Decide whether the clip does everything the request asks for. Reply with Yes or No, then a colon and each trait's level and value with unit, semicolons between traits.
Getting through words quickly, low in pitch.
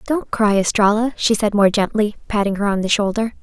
No: fast, 210 wpm; high, 210 Hz